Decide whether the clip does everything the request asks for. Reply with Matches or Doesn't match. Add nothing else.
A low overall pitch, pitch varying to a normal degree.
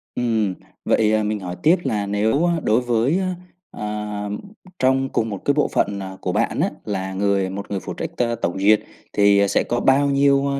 Matches